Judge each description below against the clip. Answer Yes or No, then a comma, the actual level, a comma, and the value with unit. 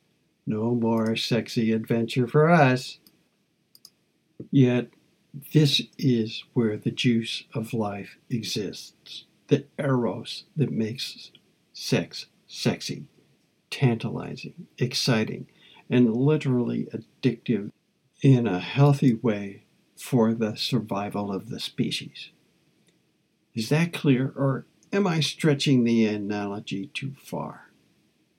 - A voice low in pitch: Yes, low, 120 Hz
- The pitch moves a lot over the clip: No, average, 3.7 semitones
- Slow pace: Yes, slow, 100 wpm